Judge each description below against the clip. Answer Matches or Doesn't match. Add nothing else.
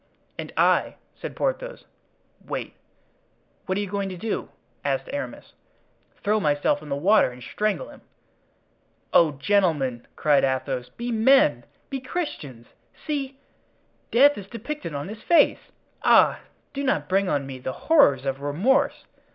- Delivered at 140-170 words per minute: Matches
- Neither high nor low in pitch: Doesn't match